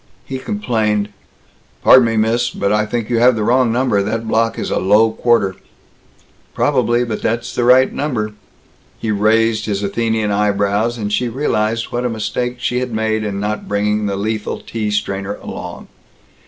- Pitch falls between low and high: No, low, 110 Hz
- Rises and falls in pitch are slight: Yes, narrow, 2.2 semitones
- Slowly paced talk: No, average, 170 wpm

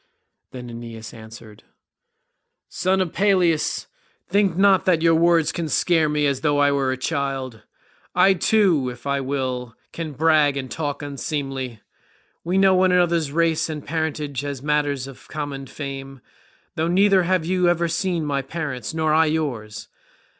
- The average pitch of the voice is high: No, medium, 150 Hz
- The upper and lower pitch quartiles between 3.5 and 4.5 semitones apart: Yes, average, 3.9 semitones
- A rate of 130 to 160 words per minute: Yes, average, 155 wpm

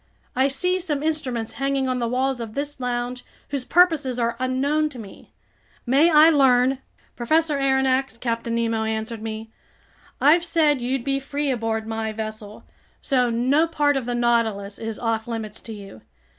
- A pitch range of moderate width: Yes, average, 3.7 semitones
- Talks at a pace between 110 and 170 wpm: Yes, average, 165 wpm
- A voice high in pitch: Yes, very high, 250 Hz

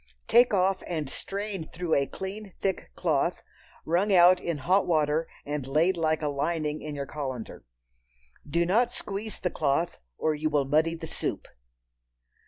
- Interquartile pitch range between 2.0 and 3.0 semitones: No, average, 4.1 semitones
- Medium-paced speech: Yes, average, 160 wpm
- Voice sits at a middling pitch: Yes, medium, 165 Hz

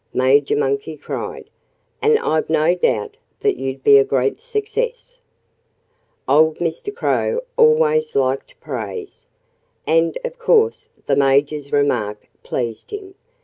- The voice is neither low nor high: Yes, medium, 160 Hz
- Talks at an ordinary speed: No, slow, 120 wpm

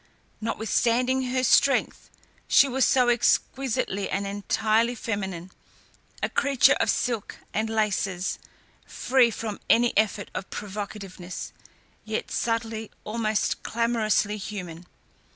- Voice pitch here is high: Yes, high, 220 Hz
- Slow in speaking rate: Yes, slow, 105 wpm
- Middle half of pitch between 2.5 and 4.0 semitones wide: Yes, average, 2.8 semitones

